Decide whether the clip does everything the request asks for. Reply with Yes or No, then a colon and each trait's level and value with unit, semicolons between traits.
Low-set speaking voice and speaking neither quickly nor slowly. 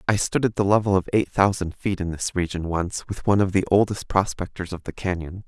No: very low, 95 Hz; fast, 240 wpm